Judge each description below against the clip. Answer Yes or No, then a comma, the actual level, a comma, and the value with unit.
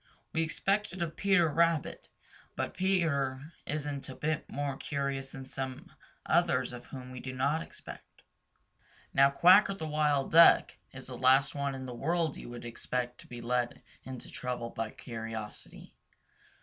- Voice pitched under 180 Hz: Yes, medium, 140 Hz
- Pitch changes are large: No, average, 3.9 semitones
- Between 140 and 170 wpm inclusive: Yes, average, 160 wpm